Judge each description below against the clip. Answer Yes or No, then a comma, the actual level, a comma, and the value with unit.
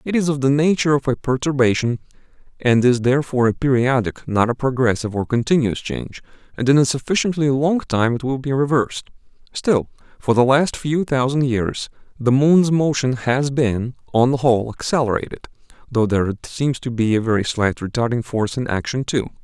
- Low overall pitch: Yes, low, 130 Hz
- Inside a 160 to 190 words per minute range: Yes, average, 180 wpm